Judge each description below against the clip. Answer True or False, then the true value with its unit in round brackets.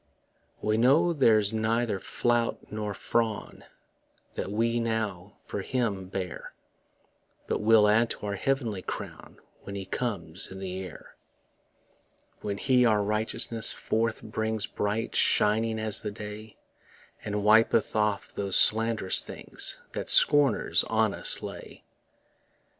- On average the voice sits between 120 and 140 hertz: False (110 Hz)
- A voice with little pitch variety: True (2.1 semitones)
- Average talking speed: False (125 wpm)